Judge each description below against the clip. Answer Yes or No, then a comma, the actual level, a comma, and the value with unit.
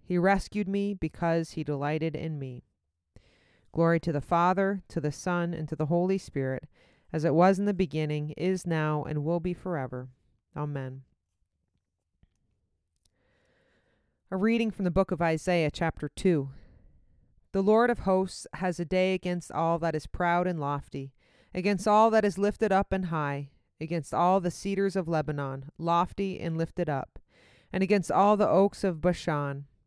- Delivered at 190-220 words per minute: No, average, 165 wpm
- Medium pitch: Yes, medium, 165 Hz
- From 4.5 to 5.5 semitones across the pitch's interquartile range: Yes, average, 5.2 semitones